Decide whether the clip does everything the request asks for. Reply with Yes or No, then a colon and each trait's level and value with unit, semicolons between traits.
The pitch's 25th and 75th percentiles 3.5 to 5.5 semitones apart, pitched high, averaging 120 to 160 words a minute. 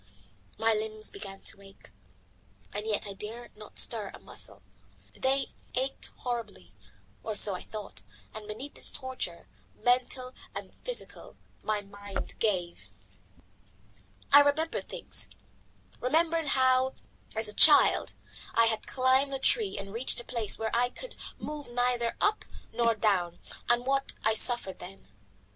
Yes: average, 3.9 semitones; high, 230 Hz; average, 140 wpm